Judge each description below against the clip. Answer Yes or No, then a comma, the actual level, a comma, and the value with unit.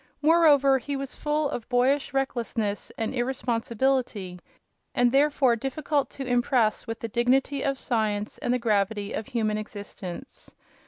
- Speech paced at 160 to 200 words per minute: No, average, 140 wpm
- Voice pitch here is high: Yes, high, 245 Hz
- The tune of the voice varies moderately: Yes, average, 3.6 semitones